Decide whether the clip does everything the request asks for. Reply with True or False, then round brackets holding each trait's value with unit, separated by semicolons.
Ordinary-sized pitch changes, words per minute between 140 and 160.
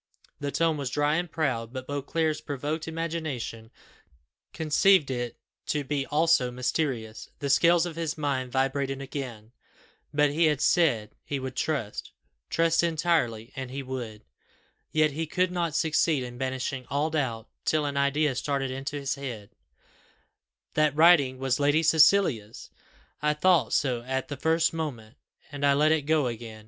True (3.5 semitones; 155 wpm)